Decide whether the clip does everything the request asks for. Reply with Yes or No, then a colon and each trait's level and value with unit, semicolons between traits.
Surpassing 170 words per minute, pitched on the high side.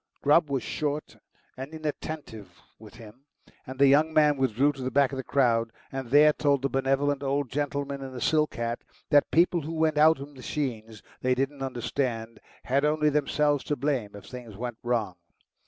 No: average, 185 wpm; low, 135 Hz